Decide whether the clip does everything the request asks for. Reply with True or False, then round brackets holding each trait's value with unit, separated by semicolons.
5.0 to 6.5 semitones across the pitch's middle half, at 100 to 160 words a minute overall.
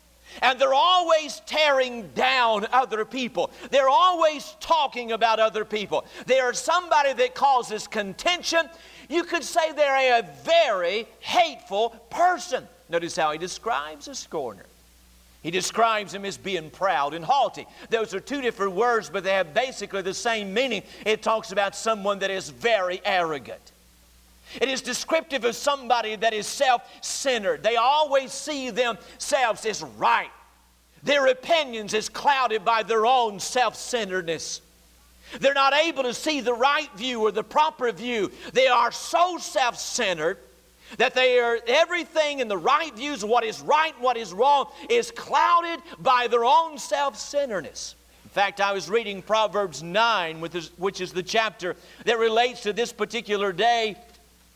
True (5.5 semitones; 155 wpm)